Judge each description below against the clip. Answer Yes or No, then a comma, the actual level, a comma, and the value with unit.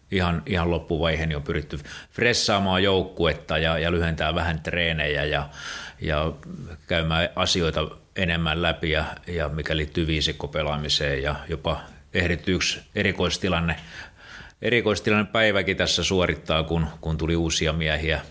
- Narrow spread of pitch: Yes, narrow, 2.1 semitones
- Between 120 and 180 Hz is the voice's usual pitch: No, very low, 85 Hz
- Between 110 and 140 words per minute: Yes, average, 120 wpm